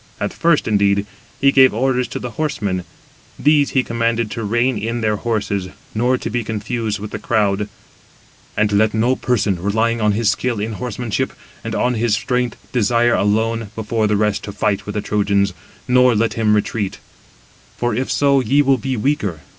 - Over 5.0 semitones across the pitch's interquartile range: No, average, 3.1 semitones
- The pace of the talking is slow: No, average, 180 wpm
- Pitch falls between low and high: No, low, 115 Hz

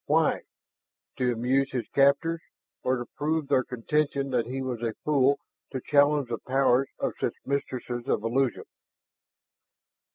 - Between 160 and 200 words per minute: No, average, 140 wpm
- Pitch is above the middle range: No, low, 135 Hz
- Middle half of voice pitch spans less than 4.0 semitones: Yes, narrow, 2.4 semitones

